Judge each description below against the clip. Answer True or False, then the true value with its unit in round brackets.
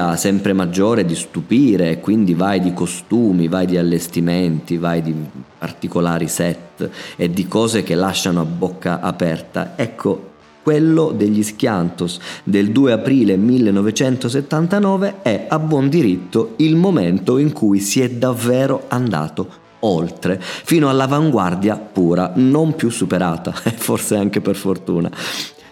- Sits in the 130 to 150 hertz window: False (100 Hz)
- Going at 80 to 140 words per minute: True (130 wpm)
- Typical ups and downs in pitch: False (6.7 semitones)